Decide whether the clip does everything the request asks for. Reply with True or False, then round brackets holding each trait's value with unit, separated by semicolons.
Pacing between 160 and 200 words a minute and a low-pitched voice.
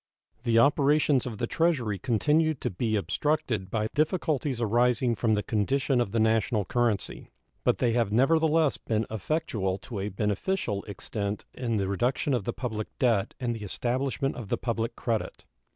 True (165 wpm; 115 Hz)